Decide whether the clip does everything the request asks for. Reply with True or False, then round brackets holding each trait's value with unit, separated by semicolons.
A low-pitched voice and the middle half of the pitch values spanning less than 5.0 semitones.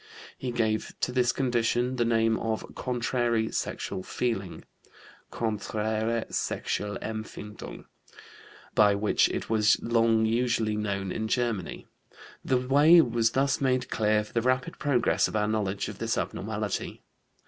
True (115 Hz; 2.4 semitones)